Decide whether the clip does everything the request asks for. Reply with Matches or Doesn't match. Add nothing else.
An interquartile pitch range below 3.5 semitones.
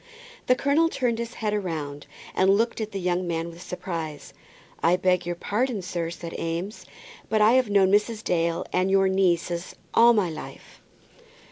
Doesn't match